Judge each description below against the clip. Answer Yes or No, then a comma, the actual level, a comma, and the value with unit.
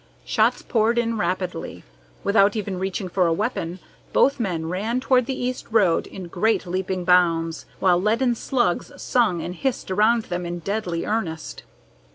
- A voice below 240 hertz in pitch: Yes, high, 190 Hz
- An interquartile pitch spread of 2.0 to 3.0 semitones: No, average, 4.5 semitones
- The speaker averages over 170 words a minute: No, average, 160 wpm